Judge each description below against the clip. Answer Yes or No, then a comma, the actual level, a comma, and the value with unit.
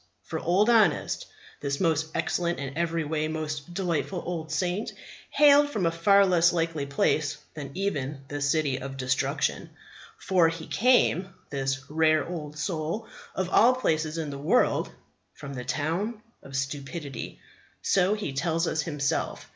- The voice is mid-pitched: Yes, medium, 160 Hz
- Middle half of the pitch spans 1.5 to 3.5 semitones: No, average, 4.0 semitones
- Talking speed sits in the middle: Yes, average, 150 wpm